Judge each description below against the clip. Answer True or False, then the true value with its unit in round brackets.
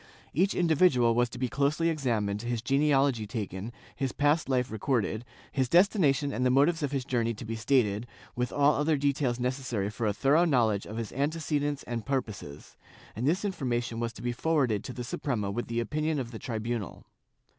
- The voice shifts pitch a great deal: False (3.8 semitones)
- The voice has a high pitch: False (125 Hz)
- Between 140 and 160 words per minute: False (190 wpm)